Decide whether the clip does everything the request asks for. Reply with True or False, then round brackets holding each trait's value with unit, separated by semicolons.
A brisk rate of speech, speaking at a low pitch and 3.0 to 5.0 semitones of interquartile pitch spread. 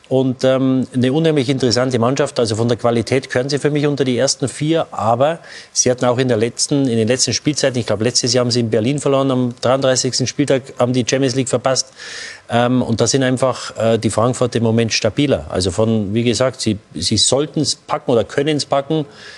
False (215 wpm; 125 Hz; 2.4 semitones)